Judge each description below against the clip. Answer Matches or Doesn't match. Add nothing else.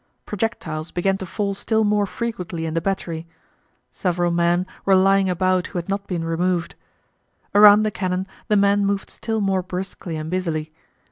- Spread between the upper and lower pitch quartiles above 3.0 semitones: Doesn't match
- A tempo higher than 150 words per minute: Matches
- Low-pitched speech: Doesn't match